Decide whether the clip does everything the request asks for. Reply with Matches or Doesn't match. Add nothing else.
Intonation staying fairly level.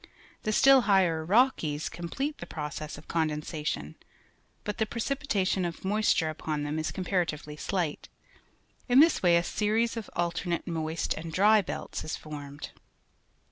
Doesn't match